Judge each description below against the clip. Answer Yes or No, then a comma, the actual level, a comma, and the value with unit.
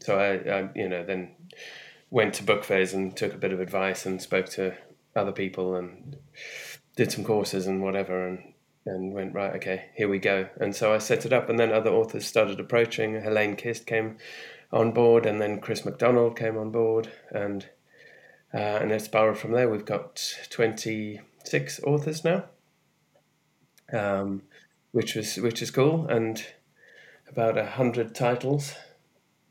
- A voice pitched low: Yes, low, 110 Hz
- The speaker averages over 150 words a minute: Yes, average, 165 wpm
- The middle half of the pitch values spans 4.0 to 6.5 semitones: No, average, 3.3 semitones